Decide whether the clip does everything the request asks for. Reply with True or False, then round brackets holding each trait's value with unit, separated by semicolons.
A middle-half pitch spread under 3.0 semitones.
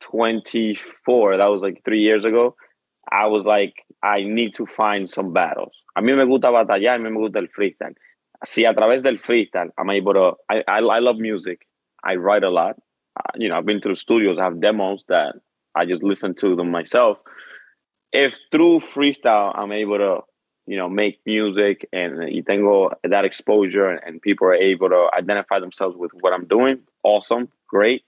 True (2.5 semitones)